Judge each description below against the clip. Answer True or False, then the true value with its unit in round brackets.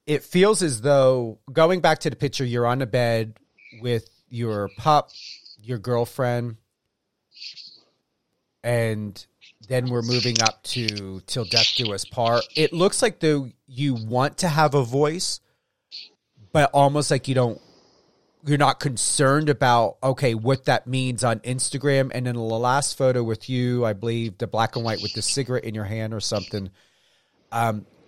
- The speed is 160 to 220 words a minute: True (165 wpm)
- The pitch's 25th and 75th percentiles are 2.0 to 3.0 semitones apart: False (3.6 semitones)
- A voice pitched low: True (125 Hz)